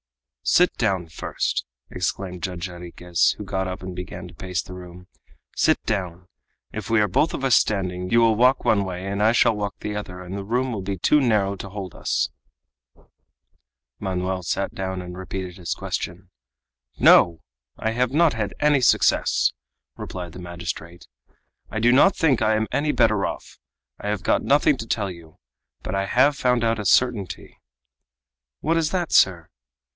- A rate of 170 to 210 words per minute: Yes, average, 180 wpm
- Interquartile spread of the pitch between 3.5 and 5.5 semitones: Yes, average, 4.0 semitones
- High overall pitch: No, low, 100 Hz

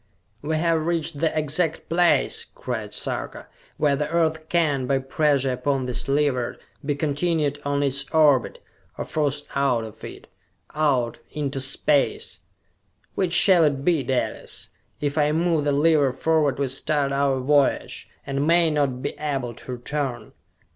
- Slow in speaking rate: No, average, 155 wpm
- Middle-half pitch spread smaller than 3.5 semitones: Yes, narrow, 2.5 semitones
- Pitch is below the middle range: No, medium, 145 Hz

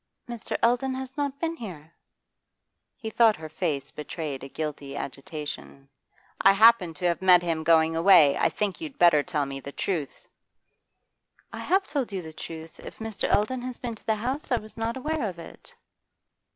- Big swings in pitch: Yes, wide, 7.1 semitones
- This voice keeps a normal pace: Yes, average, 180 wpm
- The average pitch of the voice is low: No, medium, 185 Hz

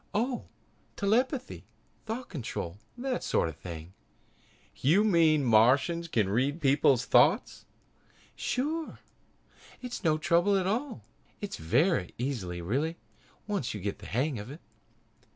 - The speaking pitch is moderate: Yes, medium, 155 Hz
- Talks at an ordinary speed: No, slow, 130 wpm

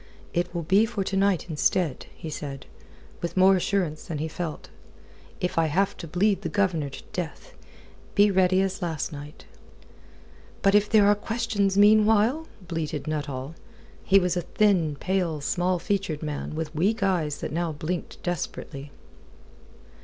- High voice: No, medium, 180 Hz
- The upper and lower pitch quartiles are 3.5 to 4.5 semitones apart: Yes, average, 4.2 semitones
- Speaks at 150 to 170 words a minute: Yes, average, 155 wpm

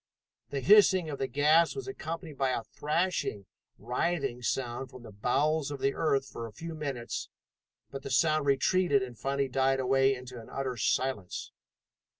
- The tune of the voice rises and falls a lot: No, average, 3.5 semitones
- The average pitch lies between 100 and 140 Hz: Yes, low, 135 Hz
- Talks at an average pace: Yes, average, 165 wpm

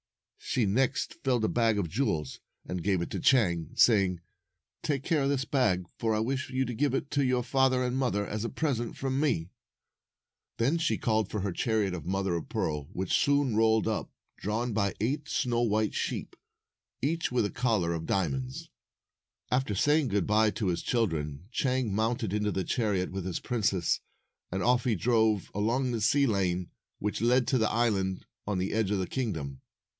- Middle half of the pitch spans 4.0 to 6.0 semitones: Yes, average, 4.9 semitones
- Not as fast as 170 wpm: No, average, 195 wpm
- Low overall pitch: Yes, low, 110 Hz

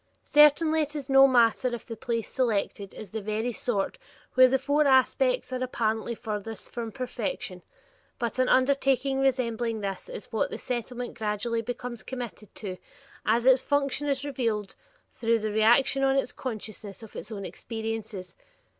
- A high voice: Yes, high, 240 Hz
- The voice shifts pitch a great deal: No, average, 3.5 semitones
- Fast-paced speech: No, average, 165 wpm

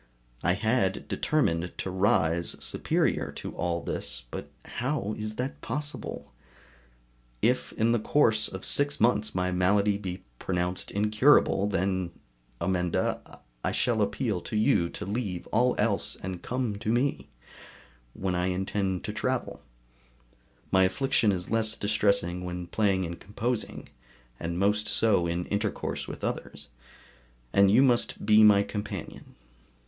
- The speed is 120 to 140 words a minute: Yes, slow, 135 wpm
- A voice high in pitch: No, low, 100 Hz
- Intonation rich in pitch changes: No, average, 3.4 semitones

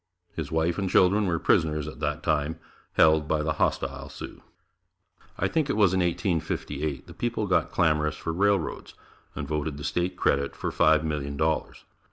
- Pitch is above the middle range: No, very low, 80 Hz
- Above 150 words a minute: Yes, average, 175 wpm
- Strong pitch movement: No, average, 2.9 semitones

